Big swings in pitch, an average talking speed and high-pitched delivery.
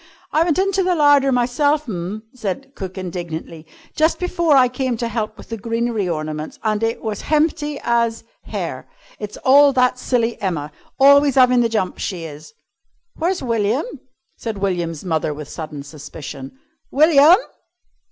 Yes: wide, 7.7 semitones; average, 160 wpm; high, 230 Hz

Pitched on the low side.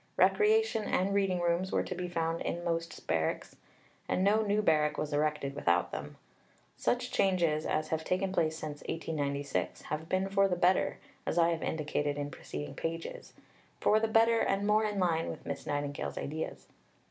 No: medium, 165 Hz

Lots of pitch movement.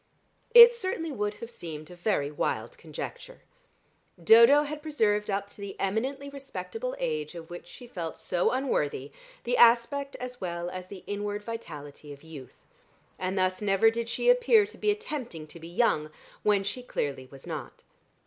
Yes: wide, 8.3 semitones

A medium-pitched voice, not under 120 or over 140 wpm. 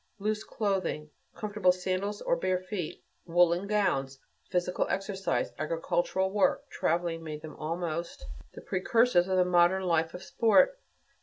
Yes: medium, 180 Hz; slow, 135 wpm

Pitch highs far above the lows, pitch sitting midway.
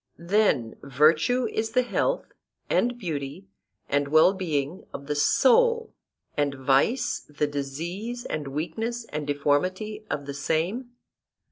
Yes: wide, 7.7 semitones; medium, 160 Hz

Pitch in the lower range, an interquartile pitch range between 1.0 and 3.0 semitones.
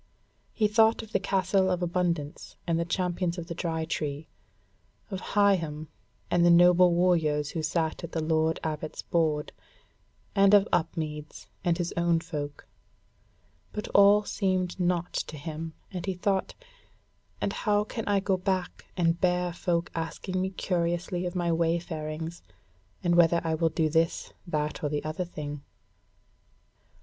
No: medium, 170 Hz; narrow, 2.4 semitones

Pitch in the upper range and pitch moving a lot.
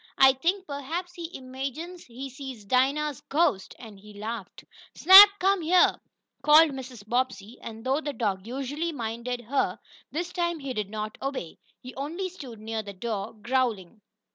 Yes: very high, 260 Hz; wide, 5.7 semitones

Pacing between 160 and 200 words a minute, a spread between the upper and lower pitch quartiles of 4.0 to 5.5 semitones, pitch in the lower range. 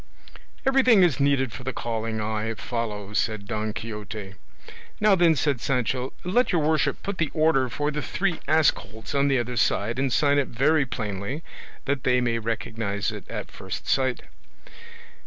Yes: average, 170 wpm; average, 5.2 semitones; low, 130 Hz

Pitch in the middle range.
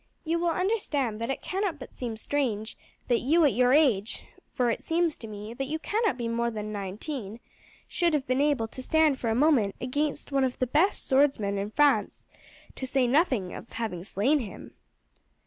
No: very high, 260 Hz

